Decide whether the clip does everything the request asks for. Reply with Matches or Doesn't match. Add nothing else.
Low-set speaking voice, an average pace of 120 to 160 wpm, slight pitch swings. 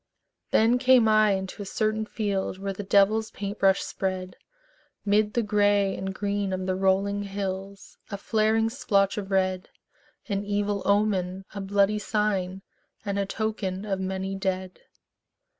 Doesn't match